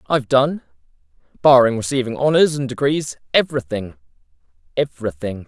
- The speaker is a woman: No, male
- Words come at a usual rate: No, slow, 65 wpm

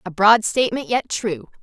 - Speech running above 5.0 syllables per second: No, 4.9 syllables/s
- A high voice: Yes, high, 215 Hz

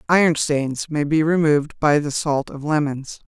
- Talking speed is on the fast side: No, average, 180 wpm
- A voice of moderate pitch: Yes, medium, 150 Hz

